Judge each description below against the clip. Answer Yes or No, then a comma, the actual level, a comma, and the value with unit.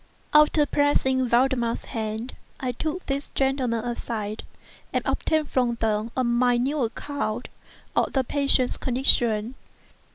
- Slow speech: Yes, slow, 120 wpm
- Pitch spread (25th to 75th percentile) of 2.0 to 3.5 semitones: Yes, average, 3.0 semitones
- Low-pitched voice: No, very high, 250 Hz